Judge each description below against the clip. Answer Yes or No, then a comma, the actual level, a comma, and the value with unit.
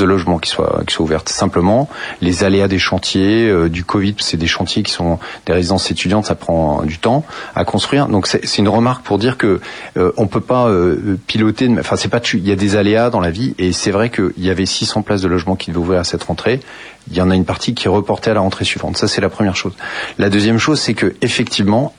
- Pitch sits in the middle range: No, low, 100 Hz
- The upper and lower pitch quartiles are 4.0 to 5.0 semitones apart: No, average, 3.4 semitones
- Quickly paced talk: Yes, fast, 260 wpm